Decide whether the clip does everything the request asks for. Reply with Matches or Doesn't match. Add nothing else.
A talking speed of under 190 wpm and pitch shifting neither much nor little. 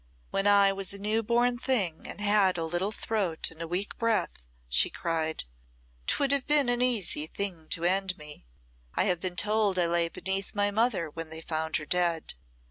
Doesn't match